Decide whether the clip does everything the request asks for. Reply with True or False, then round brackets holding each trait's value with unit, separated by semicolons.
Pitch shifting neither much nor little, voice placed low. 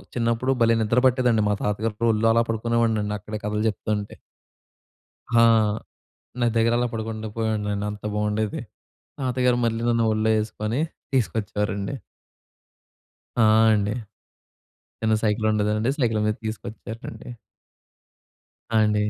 False (1.7 semitones; 110 Hz)